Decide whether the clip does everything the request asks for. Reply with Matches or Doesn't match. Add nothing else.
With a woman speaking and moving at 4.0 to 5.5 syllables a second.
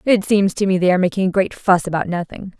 Doesn't match